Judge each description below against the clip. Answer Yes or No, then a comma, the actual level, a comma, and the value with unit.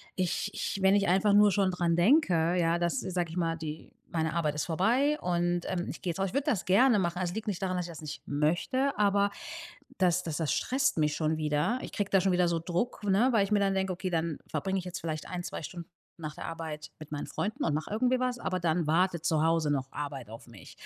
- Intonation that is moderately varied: Yes, average, 3.6 semitones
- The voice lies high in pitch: No, medium, 175 Hz